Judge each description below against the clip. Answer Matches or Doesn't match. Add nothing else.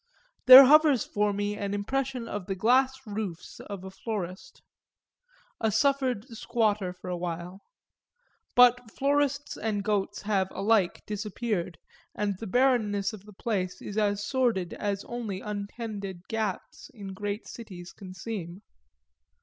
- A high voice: Matches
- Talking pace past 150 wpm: Doesn't match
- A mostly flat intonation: Doesn't match